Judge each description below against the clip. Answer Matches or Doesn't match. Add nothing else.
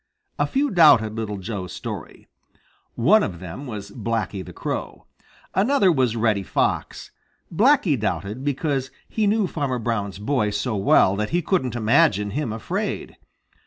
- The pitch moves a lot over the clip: Matches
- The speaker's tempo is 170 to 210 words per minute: Doesn't match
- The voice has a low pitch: Matches